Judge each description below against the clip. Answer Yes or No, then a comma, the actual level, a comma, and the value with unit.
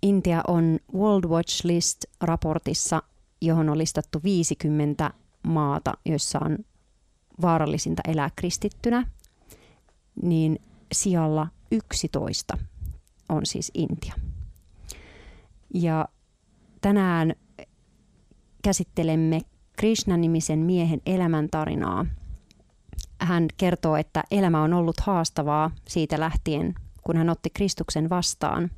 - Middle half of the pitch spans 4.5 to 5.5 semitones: No, average, 2.7 semitones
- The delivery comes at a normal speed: No, slow, 85 wpm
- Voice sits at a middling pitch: Yes, medium, 160 Hz